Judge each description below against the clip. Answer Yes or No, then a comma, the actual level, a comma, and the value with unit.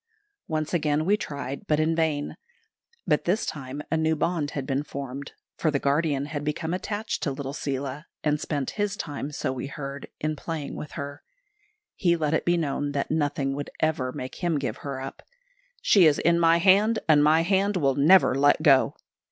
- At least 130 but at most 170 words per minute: No, average, 195 wpm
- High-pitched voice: No, medium, 150 Hz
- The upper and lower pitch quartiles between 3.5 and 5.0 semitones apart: No, average, 2.8 semitones